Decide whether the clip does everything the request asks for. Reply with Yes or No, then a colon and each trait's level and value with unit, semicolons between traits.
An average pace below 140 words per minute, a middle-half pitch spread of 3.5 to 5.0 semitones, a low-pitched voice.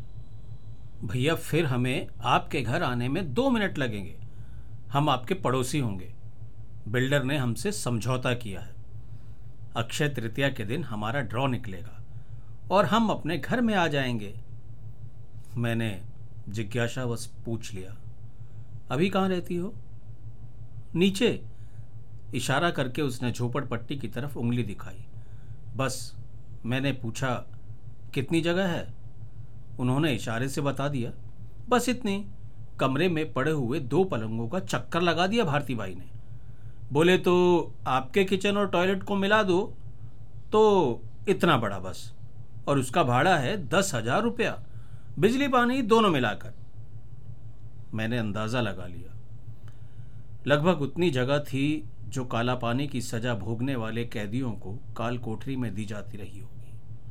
Yes: average, 130 wpm; average, 4.0 semitones; low, 120 Hz